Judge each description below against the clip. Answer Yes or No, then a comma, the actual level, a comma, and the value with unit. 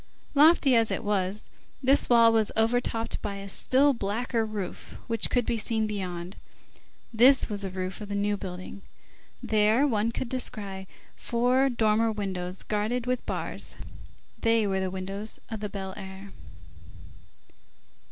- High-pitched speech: Yes, high, 215 Hz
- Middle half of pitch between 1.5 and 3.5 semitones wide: Yes, average, 3.1 semitones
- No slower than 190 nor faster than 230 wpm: No, average, 145 wpm